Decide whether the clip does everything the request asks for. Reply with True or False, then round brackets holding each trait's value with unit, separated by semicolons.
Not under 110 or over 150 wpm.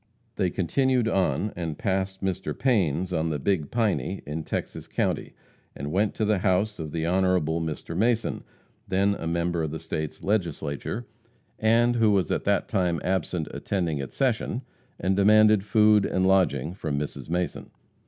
False (165 wpm)